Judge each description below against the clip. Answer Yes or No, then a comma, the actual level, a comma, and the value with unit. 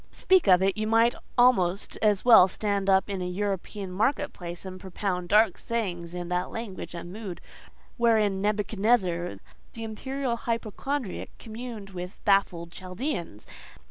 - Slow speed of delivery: No, average, 145 wpm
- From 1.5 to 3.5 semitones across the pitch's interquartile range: No, average, 3.9 semitones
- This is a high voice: Yes, high, 200 Hz